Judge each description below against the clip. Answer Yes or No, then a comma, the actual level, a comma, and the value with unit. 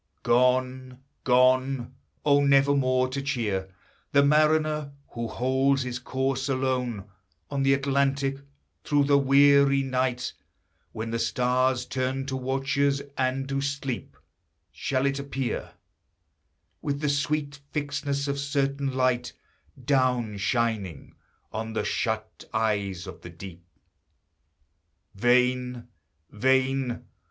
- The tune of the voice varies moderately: No, narrow, 2.1 semitones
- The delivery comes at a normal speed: No, slow, 110 wpm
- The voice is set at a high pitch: No, low, 130 Hz